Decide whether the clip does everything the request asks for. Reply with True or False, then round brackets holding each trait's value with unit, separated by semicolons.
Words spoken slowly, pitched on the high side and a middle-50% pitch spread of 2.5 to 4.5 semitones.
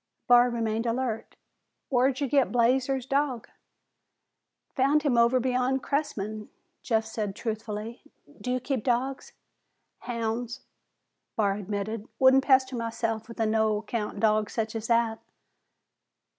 True (125 wpm; 235 Hz; 2.8 semitones)